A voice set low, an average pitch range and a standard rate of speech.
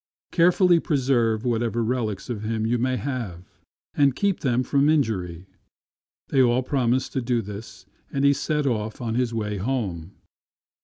Yes: low, 120 Hz; average, 3.7 semitones; average, 160 wpm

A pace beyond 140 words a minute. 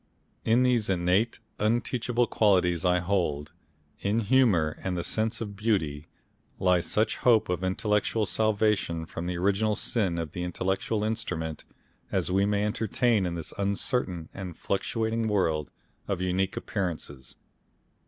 No: slow, 135 wpm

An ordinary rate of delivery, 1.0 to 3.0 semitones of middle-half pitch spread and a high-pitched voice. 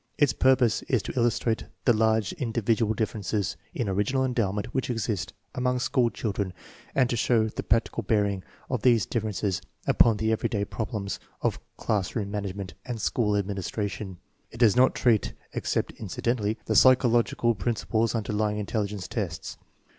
No: average, 150 wpm; average, 2.7 semitones; low, 110 Hz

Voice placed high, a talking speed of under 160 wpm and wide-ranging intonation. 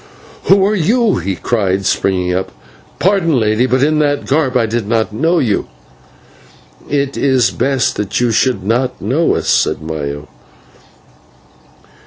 No: low, 125 Hz; average, 145 wpm; wide, 6.3 semitones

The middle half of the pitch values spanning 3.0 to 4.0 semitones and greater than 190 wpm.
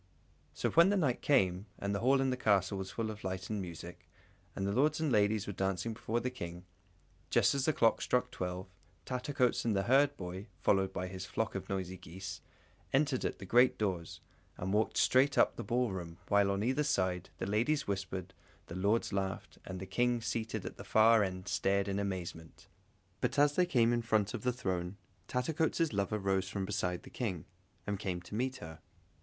No: average, 4.9 semitones; average, 200 wpm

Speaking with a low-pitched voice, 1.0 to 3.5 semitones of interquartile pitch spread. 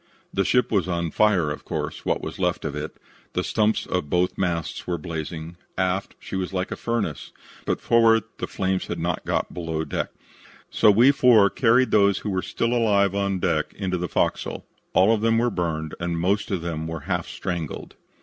No: very low, 95 Hz; average, 3.9 semitones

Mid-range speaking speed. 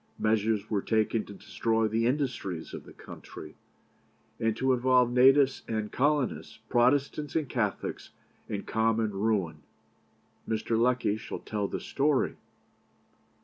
No: slow, 125 wpm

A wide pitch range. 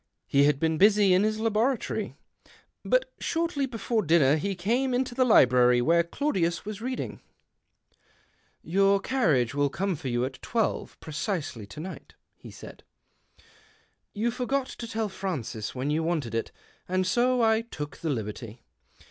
Yes: wide, 8.0 semitones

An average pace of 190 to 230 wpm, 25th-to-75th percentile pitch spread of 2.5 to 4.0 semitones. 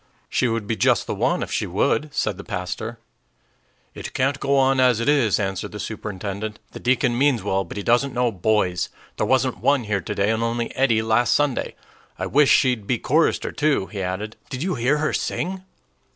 No: average, 200 wpm; average, 4.4 semitones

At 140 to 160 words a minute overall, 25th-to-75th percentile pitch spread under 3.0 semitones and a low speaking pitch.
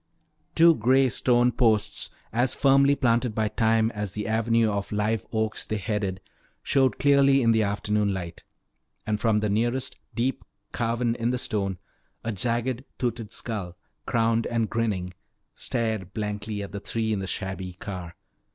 Yes: average, 155 wpm; narrow, 2.6 semitones; low, 110 Hz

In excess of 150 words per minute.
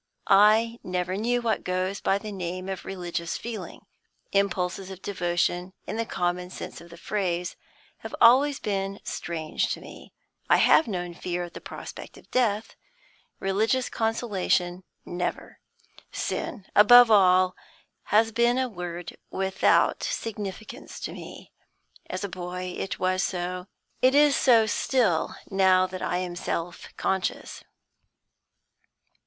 No: slow, 135 wpm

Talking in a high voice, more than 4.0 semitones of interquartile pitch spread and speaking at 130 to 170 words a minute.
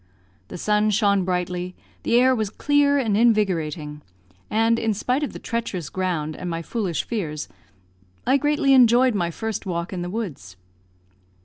Yes: high, 205 Hz; average, 5.0 semitones; average, 155 wpm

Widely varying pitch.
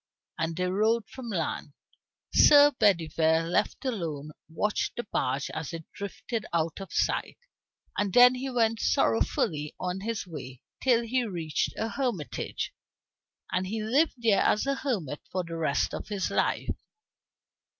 Yes: wide, 6.2 semitones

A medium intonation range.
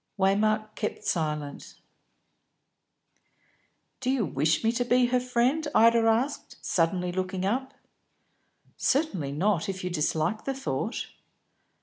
No: wide, 5.7 semitones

